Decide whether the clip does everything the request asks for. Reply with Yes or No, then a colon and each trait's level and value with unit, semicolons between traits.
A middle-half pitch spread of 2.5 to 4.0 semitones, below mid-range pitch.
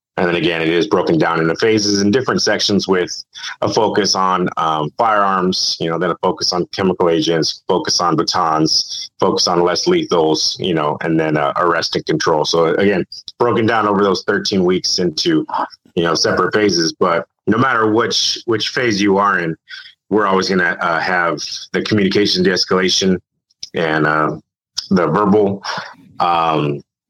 Yes: average, 3.7 semitones; very low, 90 Hz